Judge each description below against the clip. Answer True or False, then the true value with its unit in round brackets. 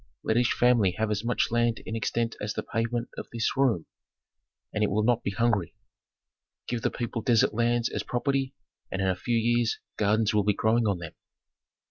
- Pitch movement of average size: False (2.1 semitones)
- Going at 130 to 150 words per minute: False (195 wpm)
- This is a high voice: False (115 Hz)